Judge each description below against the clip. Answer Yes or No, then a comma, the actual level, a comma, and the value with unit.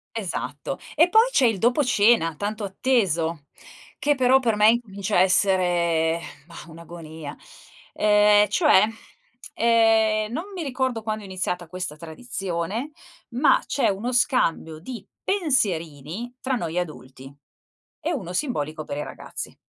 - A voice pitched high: Yes, high, 210 Hz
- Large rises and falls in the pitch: Yes, wide, 6.4 semitones